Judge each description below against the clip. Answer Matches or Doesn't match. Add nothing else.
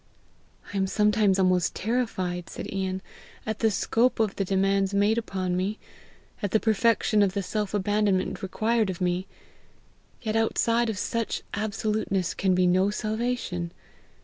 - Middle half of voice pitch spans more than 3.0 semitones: Doesn't match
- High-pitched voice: Matches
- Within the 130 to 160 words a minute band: Matches